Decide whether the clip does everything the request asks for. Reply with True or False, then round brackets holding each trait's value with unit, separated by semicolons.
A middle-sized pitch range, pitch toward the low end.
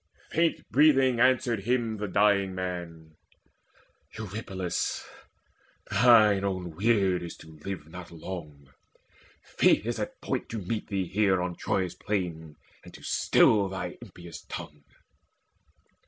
True (3.8 semitones; 95 Hz)